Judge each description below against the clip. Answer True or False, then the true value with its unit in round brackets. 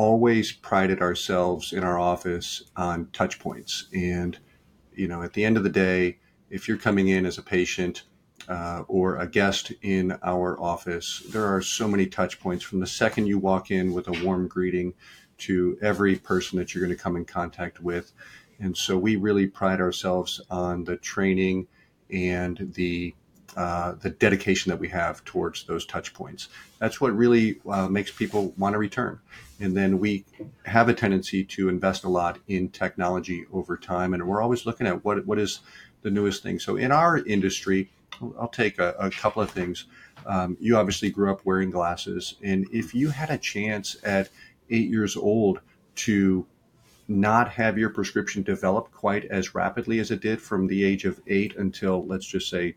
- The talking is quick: False (185 wpm)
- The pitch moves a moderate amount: False (2.3 semitones)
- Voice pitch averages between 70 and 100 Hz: True (95 Hz)